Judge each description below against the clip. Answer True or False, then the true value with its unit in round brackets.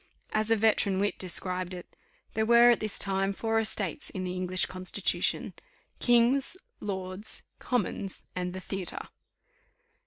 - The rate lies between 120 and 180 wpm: True (135 wpm)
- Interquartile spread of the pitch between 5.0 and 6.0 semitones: False (3.3 semitones)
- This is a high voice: True (195 Hz)